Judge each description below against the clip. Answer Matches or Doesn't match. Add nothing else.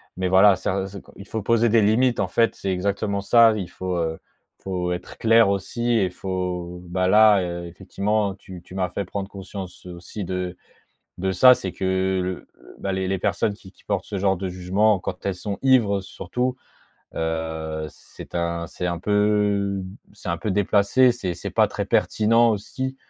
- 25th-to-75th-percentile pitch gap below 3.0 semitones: Matches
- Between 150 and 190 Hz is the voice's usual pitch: Doesn't match